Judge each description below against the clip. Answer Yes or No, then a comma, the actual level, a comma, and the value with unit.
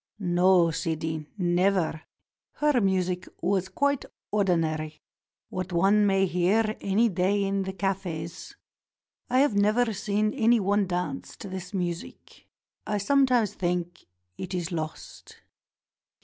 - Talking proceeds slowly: Yes, slow, 120 wpm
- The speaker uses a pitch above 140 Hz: Yes, high, 190 Hz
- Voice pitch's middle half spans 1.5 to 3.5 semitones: Yes, average, 3.0 semitones